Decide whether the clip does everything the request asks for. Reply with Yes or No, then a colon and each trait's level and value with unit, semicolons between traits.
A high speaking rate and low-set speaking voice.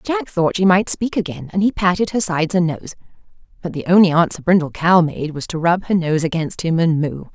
No: fast, 235 wpm; medium, 175 Hz